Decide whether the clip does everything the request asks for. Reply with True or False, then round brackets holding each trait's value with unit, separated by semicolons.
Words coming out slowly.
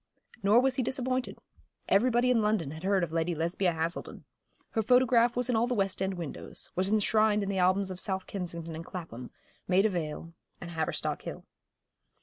False (180 wpm)